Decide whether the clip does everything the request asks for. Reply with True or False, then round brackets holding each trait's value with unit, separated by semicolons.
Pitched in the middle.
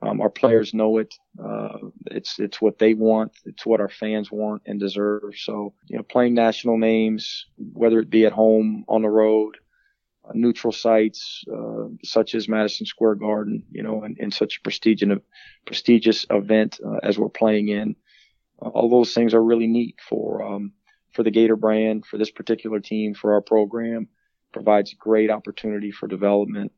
False (110 Hz)